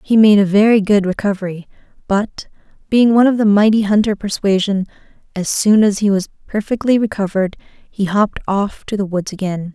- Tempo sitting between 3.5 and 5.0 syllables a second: No, 5.5 syllables/s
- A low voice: No, high, 205 Hz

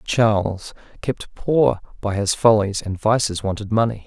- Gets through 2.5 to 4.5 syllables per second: Yes, 4.3 syllables/s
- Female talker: No, male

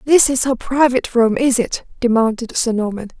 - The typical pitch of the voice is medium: No, high, 245 Hz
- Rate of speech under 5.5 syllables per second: Yes, 5.3 syllables/s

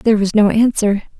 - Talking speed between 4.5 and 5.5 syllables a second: No, 5.9 syllables/s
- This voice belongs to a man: No, female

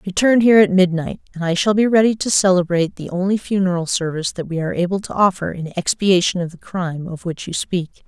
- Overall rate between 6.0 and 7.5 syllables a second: Yes, 6.2 syllables/s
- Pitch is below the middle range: No, medium, 185 Hz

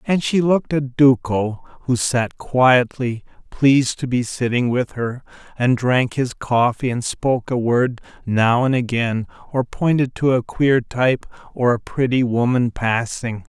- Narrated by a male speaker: Yes, male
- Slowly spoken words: No, average, 160 wpm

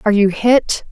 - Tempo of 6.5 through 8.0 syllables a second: No, 5.1 syllables/s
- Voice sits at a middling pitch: No, high, 215 Hz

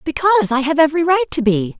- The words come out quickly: Yes, fast, 235 wpm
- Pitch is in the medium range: No, very high, 295 Hz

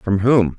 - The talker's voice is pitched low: Yes, low, 105 Hz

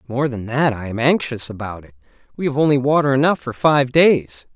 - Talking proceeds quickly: Yes, fast, 210 wpm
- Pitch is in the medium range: No, low, 130 Hz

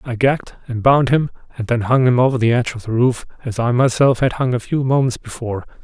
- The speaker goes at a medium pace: No, fast, 245 wpm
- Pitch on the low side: Yes, low, 125 Hz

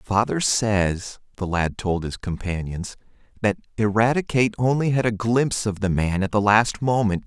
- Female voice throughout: No, male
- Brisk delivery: No, average, 165 wpm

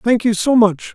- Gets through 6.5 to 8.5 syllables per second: No, 4.7 syllables/s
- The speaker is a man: Yes, male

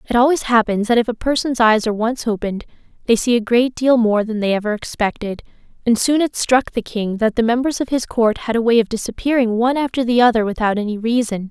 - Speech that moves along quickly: Yes, fast, 235 wpm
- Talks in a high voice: Yes, high, 230 Hz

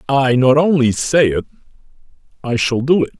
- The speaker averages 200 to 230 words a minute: No, average, 170 wpm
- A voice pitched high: No, low, 135 Hz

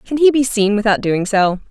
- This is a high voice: Yes, high, 220 Hz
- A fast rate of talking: Yes, fast, 245 wpm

